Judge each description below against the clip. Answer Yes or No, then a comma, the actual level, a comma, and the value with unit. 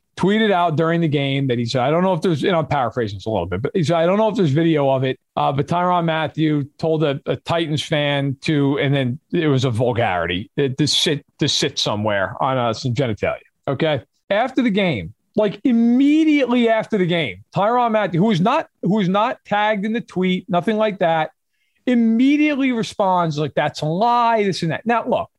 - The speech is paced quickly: Yes, fast, 215 wpm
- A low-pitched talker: No, medium, 170 Hz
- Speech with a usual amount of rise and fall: No, wide, 7.1 semitones